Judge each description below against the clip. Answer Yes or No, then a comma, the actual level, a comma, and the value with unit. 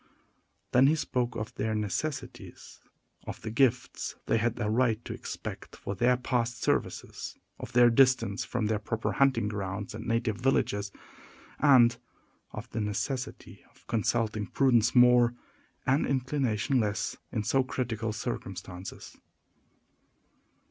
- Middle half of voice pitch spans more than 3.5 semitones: No, average, 2.9 semitones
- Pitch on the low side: Yes, low, 115 Hz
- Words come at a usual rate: No, slow, 130 wpm